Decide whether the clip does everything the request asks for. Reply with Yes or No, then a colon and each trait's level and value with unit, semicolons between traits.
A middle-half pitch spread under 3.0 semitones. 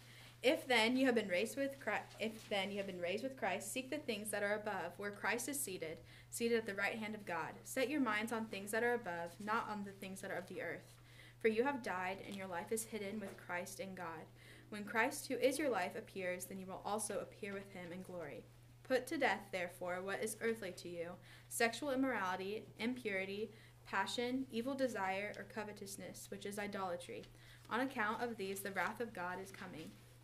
No: average, 4.2 semitones